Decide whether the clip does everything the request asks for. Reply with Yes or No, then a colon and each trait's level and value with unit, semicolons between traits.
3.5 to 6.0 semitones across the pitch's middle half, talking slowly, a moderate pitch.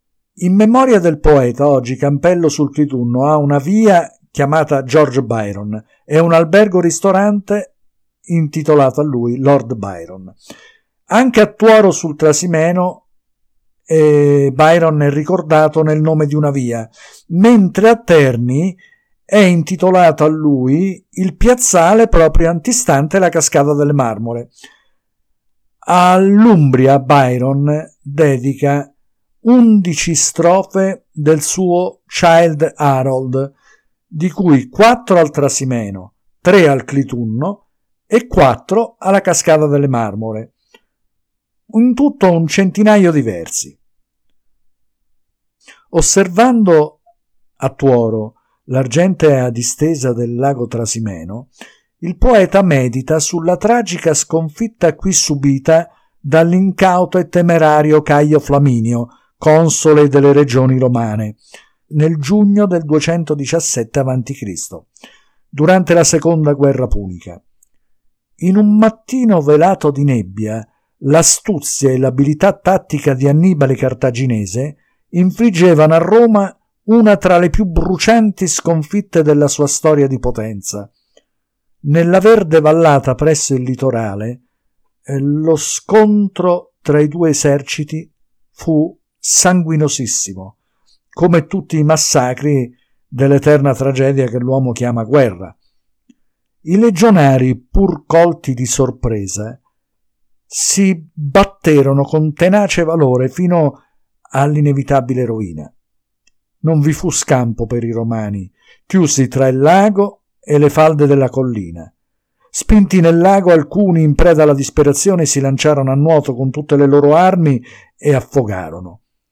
Yes: average, 5.2 semitones; slow, 110 wpm; medium, 150 Hz